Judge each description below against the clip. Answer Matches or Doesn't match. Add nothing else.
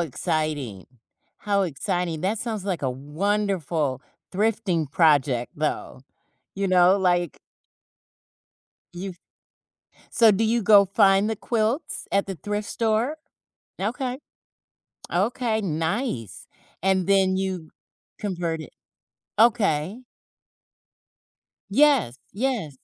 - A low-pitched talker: Doesn't match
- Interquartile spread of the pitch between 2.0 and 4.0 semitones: Doesn't match